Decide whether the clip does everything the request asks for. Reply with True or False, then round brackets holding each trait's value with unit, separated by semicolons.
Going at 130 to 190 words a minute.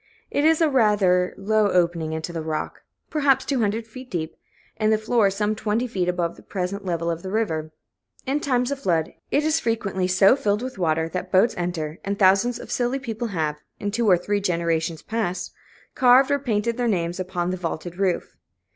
False (200 wpm)